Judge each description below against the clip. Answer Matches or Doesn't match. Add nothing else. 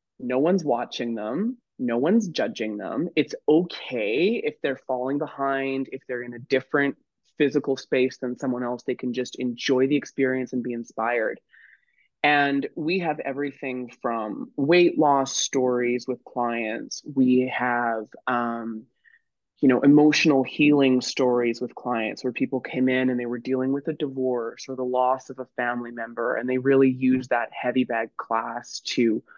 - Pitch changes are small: Matches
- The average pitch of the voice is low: Matches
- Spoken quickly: Doesn't match